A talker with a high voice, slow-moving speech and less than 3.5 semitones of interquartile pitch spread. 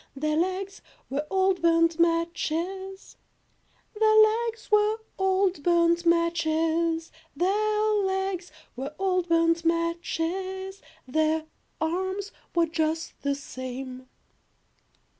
Yes: very high, 340 Hz; slow, 95 wpm; average, 2.9 semitones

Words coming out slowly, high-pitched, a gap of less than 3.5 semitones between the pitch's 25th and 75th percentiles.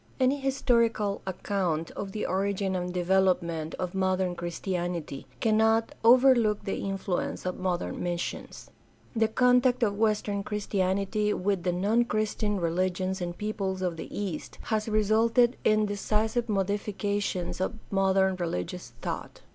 Yes: slow, 130 wpm; high, 200 Hz; average, 3.0 semitones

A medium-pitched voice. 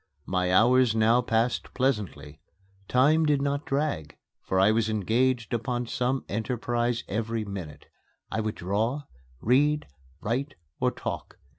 No: low, 115 Hz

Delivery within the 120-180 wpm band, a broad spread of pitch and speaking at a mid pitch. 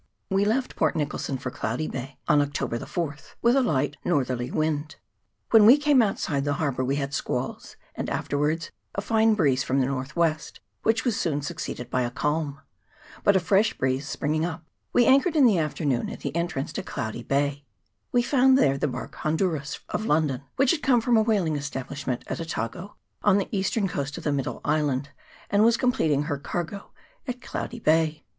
No: average, 195 wpm; wide, 6.6 semitones; medium, 155 Hz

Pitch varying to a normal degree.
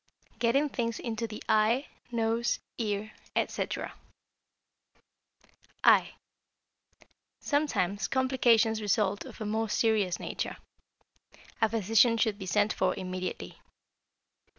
No: narrow, 2.2 semitones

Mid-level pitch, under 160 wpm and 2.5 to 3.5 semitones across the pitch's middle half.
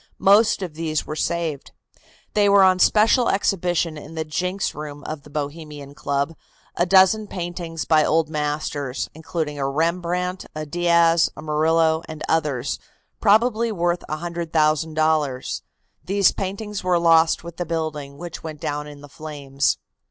Yes: medium, 160 Hz; average, 145 wpm; average, 2.8 semitones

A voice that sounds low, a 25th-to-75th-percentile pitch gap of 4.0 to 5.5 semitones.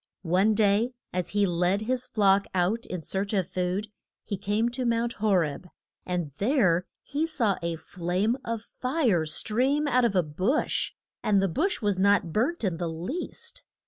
No: high, 205 Hz; average, 4.8 semitones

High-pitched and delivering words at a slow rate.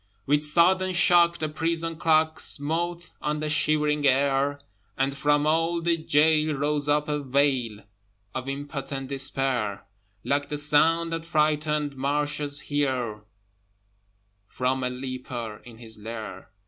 No: medium, 145 Hz; slow, 130 wpm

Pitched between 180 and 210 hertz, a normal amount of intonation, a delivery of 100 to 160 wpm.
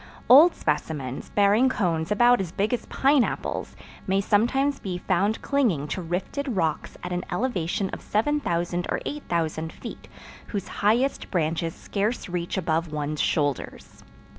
No: high, 190 Hz; wide, 6.4 semitones; average, 140 wpm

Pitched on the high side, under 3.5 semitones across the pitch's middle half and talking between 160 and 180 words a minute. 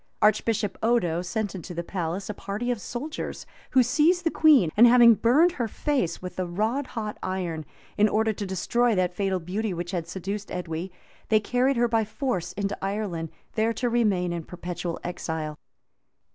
No: high, 205 Hz; average, 4.9 semitones; average, 175 wpm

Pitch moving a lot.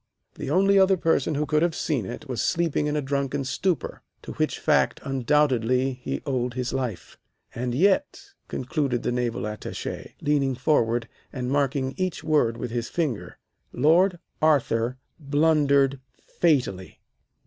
No: average, 3.8 semitones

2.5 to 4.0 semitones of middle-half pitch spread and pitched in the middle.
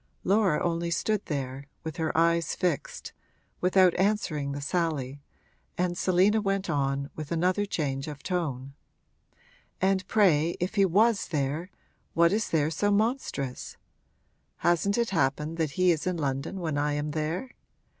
No: average, 4.6 semitones; medium, 170 Hz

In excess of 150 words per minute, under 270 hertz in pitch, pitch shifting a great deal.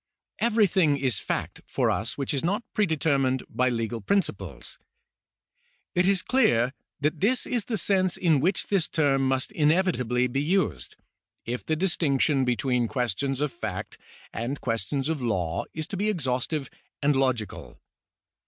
No: average, 145 wpm; medium, 140 Hz; wide, 6.4 semitones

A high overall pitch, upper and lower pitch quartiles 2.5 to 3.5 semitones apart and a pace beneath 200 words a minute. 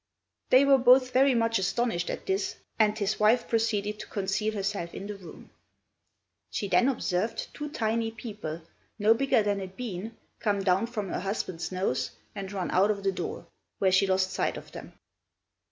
Yes: high, 205 Hz; average, 3.2 semitones; average, 180 wpm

